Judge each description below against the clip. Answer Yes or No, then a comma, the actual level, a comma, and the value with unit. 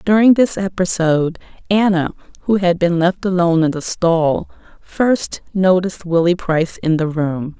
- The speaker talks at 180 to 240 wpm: No, average, 150 wpm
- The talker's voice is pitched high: No, medium, 175 Hz